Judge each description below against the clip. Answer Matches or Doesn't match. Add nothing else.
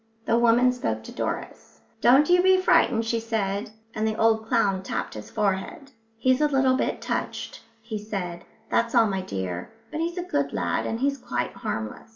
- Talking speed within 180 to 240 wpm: Matches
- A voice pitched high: Matches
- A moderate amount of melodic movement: Matches